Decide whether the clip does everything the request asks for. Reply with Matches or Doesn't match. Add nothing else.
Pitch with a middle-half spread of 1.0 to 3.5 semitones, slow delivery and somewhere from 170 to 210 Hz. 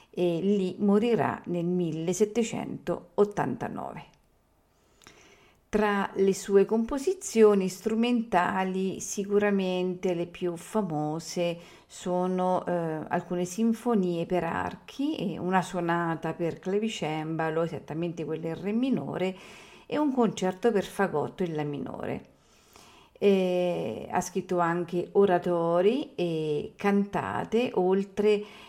Matches